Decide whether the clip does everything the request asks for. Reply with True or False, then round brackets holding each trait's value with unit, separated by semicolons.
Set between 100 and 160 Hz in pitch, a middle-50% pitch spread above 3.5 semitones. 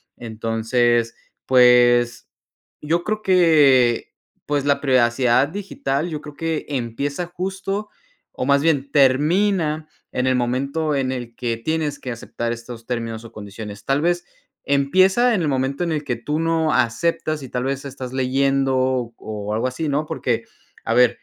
True (135 Hz; 4.5 semitones)